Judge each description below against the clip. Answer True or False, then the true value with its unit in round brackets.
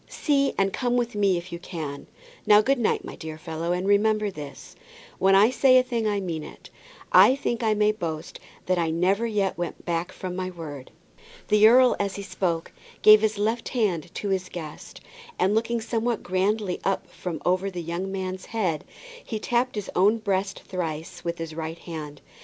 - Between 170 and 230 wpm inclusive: True (190 wpm)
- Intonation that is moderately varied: True (4.2 semitones)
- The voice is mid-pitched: False (195 Hz)